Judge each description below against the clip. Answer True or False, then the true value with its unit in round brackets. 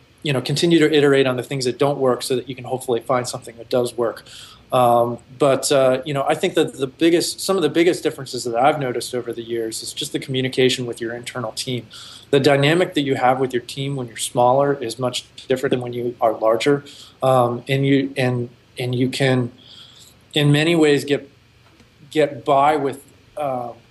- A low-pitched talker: True (130 Hz)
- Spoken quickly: True (210 wpm)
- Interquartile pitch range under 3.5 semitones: True (2.7 semitones)